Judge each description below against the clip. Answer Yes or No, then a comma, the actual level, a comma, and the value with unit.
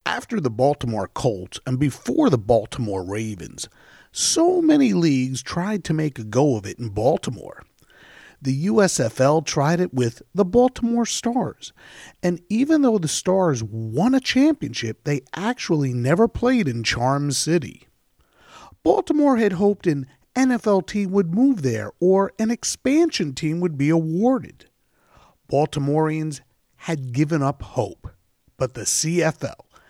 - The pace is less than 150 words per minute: Yes, slow, 135 wpm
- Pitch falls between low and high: Yes, medium, 155 Hz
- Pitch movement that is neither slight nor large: No, wide, 8.3 semitones